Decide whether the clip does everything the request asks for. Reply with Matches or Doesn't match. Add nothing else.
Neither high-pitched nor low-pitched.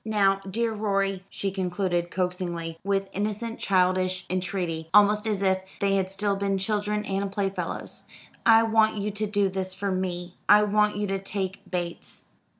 Doesn't match